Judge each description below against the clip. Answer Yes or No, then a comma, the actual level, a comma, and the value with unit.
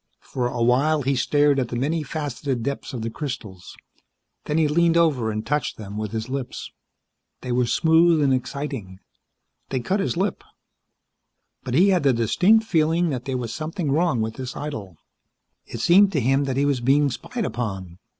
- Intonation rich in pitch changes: No, average, 4.7 semitones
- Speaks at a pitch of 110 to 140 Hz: Yes, low, 135 Hz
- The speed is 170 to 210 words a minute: Yes, average, 180 wpm